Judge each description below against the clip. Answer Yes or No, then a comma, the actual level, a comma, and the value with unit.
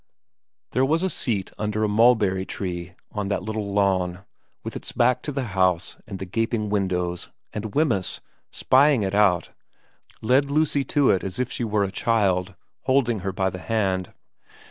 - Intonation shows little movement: No, average, 4.2 semitones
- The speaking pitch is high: No, low, 105 Hz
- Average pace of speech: Yes, average, 175 wpm